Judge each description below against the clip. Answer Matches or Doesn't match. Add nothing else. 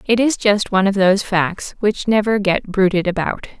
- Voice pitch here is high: Matches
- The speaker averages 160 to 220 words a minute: Matches